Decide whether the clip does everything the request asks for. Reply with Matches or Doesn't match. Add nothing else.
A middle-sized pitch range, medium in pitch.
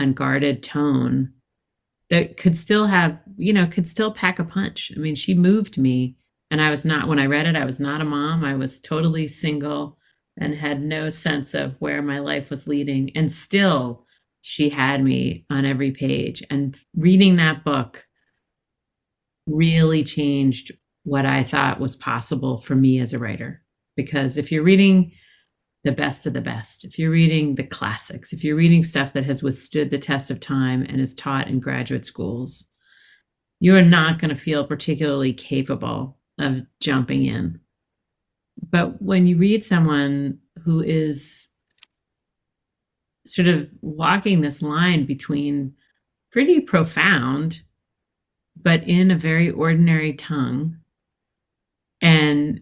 Matches